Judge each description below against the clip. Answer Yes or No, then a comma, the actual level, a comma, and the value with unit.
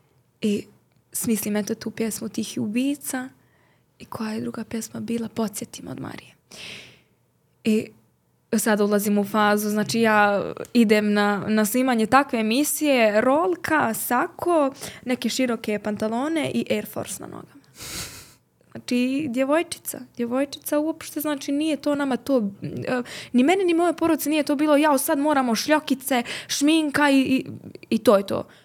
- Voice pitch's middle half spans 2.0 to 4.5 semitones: No, average, 4.9 semitones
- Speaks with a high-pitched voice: Yes, high, 245 Hz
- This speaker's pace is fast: No, average, 140 wpm